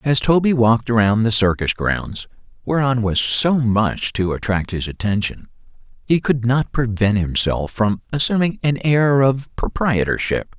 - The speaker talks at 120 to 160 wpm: Yes, average, 145 wpm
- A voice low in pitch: Yes, low, 115 Hz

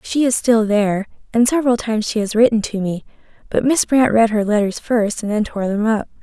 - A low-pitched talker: No, high, 220 Hz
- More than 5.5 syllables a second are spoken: Yes, 5.7 syllables/s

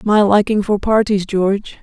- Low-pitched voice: No, high, 205 Hz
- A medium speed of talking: Yes, average, 165 wpm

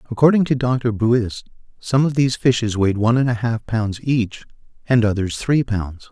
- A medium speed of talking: Yes, average, 185 wpm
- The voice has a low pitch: Yes, low, 115 Hz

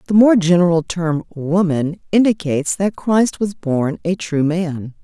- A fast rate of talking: No, average, 155 wpm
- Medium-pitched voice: Yes, medium, 175 Hz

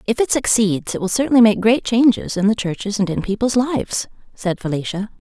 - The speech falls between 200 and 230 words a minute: Yes, fast, 205 wpm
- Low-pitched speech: No, high, 215 Hz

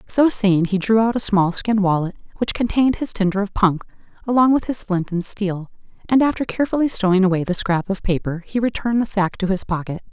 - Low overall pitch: No, high, 205 Hz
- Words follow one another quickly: Yes, fast, 220 wpm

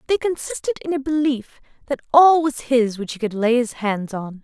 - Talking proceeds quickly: Yes, fast, 215 wpm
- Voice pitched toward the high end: Yes, very high, 265 Hz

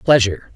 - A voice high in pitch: No, low, 110 Hz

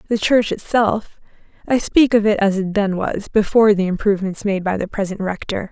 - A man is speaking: No, female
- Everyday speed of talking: Yes, average, 190 wpm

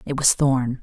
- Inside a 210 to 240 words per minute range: Yes, fast, 220 wpm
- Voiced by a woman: Yes, female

